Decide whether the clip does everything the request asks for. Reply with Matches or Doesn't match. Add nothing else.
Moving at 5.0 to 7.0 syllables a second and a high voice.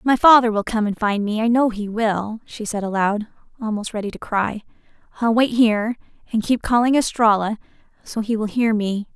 Matches